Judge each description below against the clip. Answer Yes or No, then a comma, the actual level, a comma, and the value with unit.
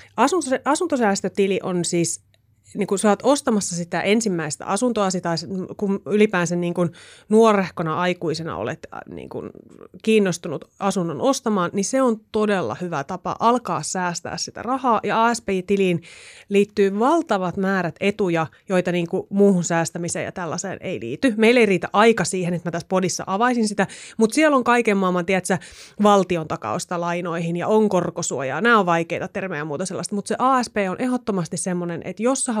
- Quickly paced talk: Yes, fast, 160 wpm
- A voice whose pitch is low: No, high, 190 Hz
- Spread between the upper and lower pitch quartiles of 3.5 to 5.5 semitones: Yes, average, 3.8 semitones